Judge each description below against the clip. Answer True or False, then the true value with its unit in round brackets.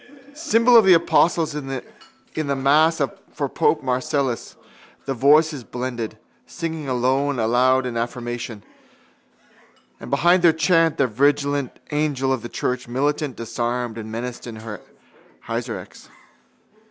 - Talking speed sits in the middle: False (120 wpm)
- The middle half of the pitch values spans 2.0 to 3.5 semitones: False (4.0 semitones)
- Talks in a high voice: False (135 Hz)